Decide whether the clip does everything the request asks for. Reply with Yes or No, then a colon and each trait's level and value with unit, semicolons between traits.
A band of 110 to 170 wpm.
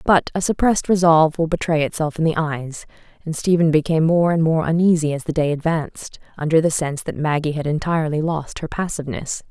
No: average, 195 wpm